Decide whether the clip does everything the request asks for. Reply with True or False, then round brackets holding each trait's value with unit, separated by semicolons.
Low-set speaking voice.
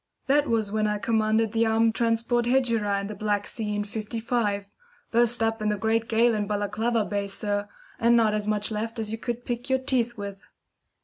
False (220 Hz)